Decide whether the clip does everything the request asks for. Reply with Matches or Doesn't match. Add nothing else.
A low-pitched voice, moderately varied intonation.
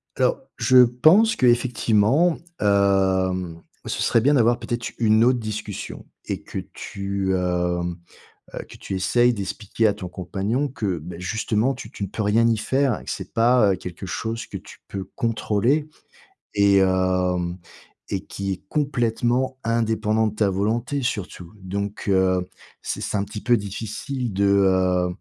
Matches